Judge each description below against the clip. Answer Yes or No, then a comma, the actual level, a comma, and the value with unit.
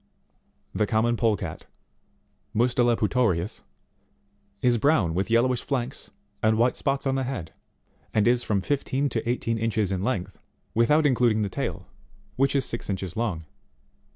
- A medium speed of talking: Yes, average, 150 wpm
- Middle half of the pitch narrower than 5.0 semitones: Yes, average, 3.5 semitones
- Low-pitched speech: Yes, low, 115 Hz